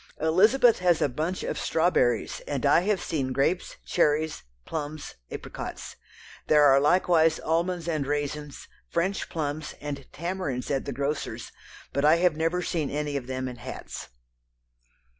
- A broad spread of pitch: No, average, 3.4 semitones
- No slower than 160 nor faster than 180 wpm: No, average, 145 wpm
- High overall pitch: No, medium, 155 Hz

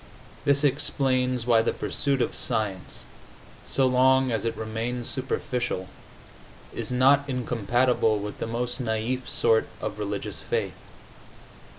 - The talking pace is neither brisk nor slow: No, slow, 120 wpm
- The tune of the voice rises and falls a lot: No, narrow, 2.5 semitones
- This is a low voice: Yes, low, 125 Hz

